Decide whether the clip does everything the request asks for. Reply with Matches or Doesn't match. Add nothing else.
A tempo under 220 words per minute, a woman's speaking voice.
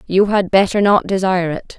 Matches